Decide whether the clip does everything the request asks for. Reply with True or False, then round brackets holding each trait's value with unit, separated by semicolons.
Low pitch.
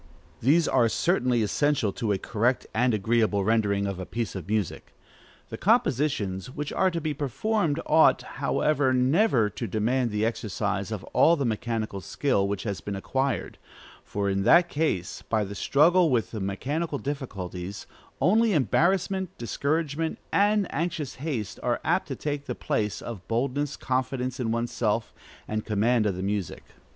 True (120 Hz)